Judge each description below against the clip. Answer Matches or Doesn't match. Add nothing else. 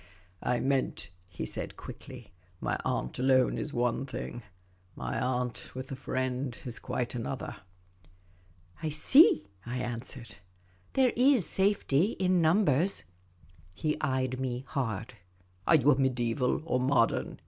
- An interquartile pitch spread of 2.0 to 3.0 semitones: Doesn't match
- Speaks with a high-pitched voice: Doesn't match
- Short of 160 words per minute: Matches